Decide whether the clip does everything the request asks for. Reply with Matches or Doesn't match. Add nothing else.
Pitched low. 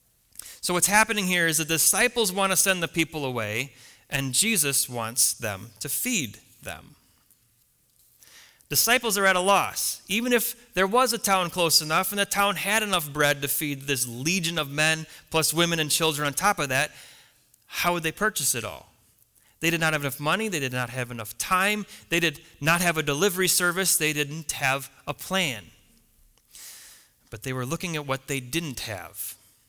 Doesn't match